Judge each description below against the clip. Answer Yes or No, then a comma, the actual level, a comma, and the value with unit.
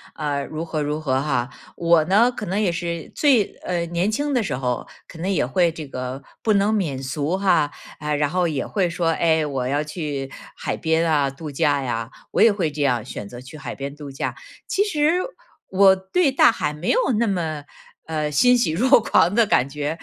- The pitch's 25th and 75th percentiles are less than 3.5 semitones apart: No, average, 5.3 semitones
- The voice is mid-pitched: Yes, medium, 160 Hz